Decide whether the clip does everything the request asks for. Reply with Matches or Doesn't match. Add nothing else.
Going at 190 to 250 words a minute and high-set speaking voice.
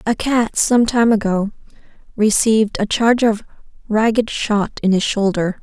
Doesn't match